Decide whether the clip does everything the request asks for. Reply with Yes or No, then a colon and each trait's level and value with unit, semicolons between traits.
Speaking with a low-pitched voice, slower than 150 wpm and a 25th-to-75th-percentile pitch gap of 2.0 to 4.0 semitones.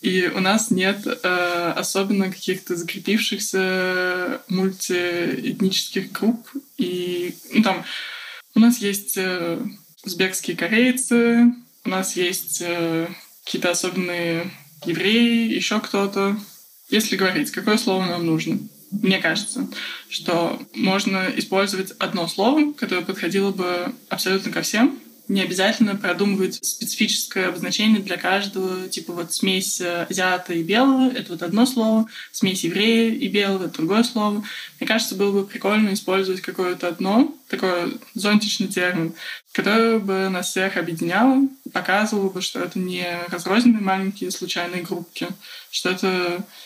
No: high, 195 Hz; average, 125 wpm; average, 3.3 semitones